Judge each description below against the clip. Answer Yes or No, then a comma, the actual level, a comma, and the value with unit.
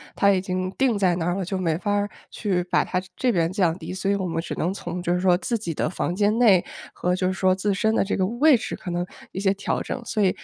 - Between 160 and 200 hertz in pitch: Yes, high, 190 Hz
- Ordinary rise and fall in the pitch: No, narrow, 2.3 semitones